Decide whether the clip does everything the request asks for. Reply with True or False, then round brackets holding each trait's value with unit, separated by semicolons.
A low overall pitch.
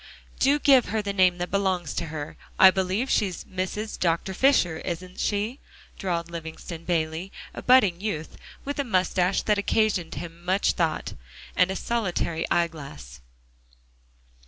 False (185 Hz)